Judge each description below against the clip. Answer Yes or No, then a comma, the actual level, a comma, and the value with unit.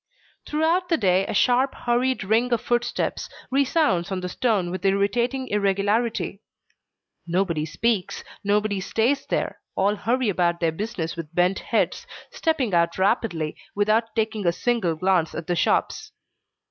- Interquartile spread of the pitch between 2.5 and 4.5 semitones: No, average, 5.0 semitones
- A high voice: Yes, high, 205 Hz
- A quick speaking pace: No, average, 145 wpm